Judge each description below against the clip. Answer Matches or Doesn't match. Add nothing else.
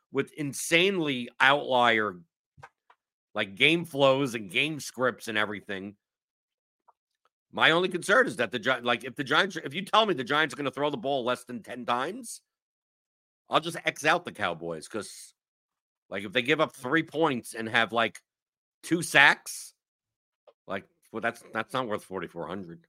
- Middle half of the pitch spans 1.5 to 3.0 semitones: Doesn't match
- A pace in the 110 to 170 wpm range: Matches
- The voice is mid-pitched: Doesn't match